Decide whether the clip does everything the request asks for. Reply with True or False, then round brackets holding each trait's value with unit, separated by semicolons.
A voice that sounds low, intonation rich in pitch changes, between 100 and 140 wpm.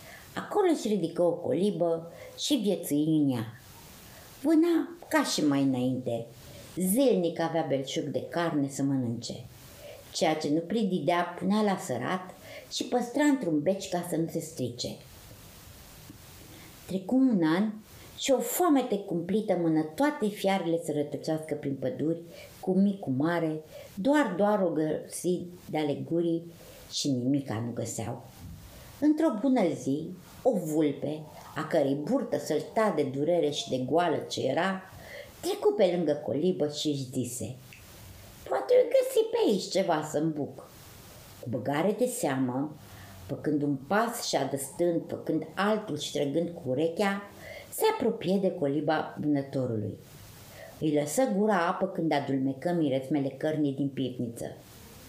False (160 Hz; 5.9 semitones; 135 wpm)